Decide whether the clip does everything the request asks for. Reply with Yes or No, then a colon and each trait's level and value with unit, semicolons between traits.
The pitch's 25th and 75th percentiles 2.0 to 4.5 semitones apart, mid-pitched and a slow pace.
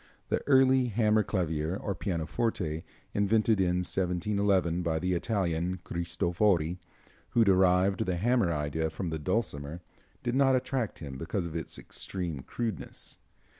No: average, 4.2 semitones; very low, 90 Hz; slow, 130 wpm